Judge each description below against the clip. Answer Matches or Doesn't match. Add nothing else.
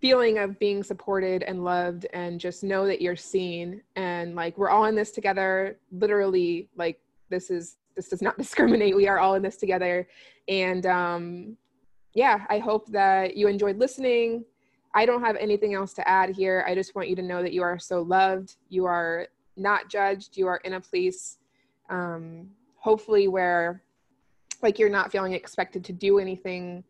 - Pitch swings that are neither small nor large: Doesn't match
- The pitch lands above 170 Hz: Matches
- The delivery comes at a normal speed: Matches